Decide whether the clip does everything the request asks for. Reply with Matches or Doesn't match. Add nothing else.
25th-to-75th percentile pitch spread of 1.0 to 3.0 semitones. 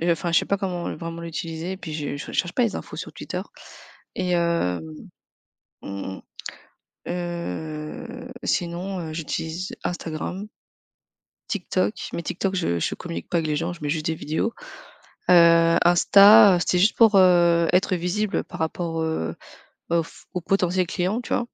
Matches